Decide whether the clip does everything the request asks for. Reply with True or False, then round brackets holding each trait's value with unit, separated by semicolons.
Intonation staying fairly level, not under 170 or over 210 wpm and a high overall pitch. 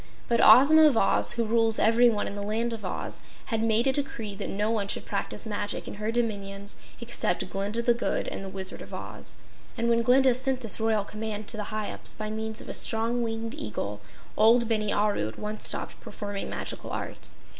True (2.3 semitones; 205 wpm; 220 Hz)